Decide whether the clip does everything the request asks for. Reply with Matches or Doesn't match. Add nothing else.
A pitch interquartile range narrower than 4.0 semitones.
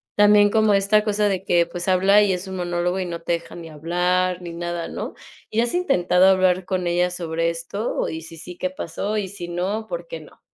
Matches